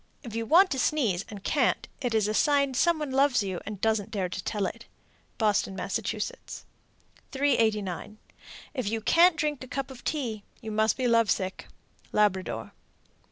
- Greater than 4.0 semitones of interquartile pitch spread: Yes, average, 4.6 semitones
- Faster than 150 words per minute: Yes, average, 170 wpm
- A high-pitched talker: Yes, high, 225 Hz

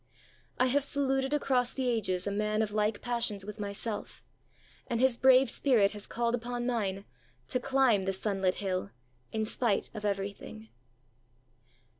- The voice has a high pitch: Yes, high, 220 Hz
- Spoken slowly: No, average, 150 wpm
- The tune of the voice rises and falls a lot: No, average, 3.7 semitones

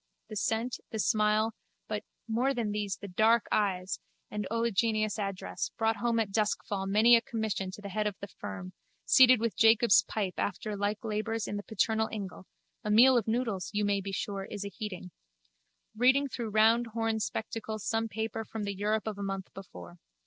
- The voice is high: Yes, high, 215 Hz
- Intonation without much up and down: Yes, narrow, 2.0 semitones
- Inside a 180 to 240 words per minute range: Yes, average, 185 wpm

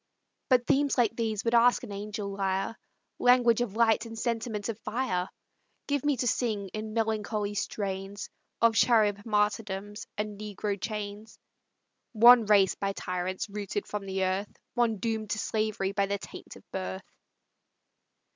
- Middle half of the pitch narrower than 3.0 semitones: Yes, narrow, 2.4 semitones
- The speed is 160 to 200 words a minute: No, average, 150 wpm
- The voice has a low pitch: No, high, 210 Hz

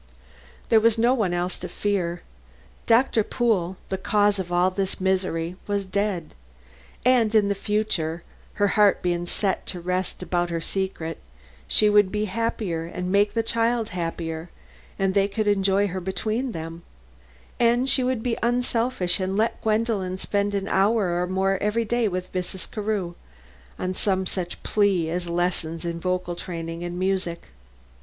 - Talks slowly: No, average, 160 wpm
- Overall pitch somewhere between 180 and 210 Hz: Yes, high, 190 Hz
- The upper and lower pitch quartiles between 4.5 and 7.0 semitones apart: No, average, 3.3 semitones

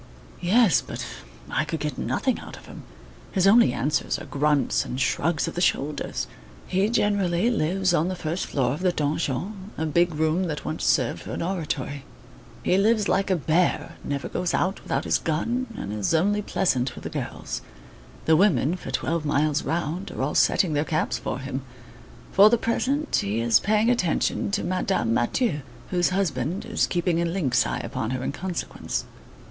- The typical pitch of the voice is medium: Yes, medium, 170 Hz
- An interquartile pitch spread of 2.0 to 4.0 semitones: No, average, 4.7 semitones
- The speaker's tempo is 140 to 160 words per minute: No, average, 185 wpm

